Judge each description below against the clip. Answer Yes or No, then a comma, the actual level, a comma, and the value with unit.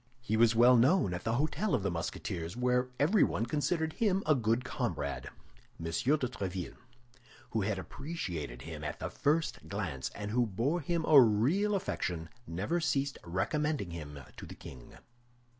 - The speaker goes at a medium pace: Yes, average, 160 wpm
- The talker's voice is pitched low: Yes, low, 115 Hz